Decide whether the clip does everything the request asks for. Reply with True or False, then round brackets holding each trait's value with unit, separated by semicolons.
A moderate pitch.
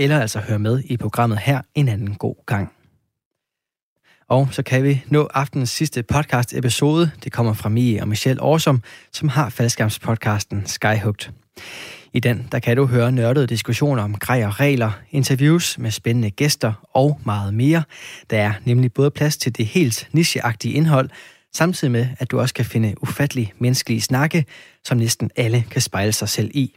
False (125 Hz)